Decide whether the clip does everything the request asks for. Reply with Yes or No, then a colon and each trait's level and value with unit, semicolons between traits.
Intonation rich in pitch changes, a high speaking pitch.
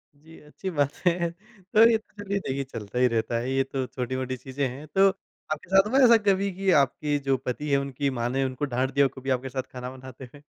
No: wide, 6.4 semitones; medium, 140 Hz